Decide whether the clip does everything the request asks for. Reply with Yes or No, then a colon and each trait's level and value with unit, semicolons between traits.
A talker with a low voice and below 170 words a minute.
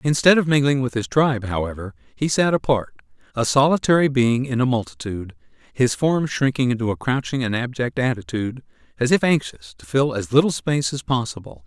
No: low, 125 Hz; average, 180 wpm